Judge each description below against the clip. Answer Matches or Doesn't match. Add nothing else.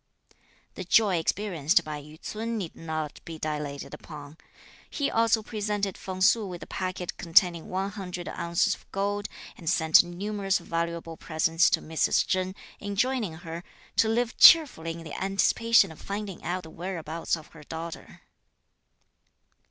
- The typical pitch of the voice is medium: Matches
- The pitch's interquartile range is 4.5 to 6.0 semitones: Doesn't match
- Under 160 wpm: Matches